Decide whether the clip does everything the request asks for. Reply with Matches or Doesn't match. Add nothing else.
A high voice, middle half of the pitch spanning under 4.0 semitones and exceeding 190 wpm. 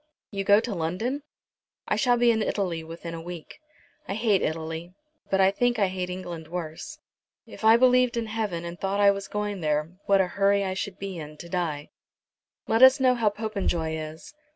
Doesn't match